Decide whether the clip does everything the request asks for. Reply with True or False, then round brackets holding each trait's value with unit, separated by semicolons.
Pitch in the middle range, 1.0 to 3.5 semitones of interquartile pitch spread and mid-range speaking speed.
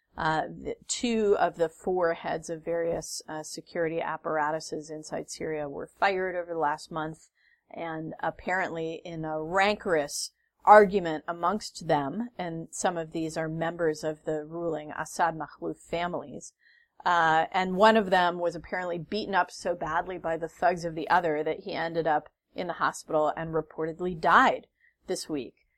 True (165 Hz; 2.6 semitones; 155 wpm)